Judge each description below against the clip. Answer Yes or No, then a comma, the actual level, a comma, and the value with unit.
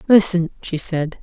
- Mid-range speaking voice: Yes, medium, 175 Hz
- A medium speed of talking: Yes, average, 145 wpm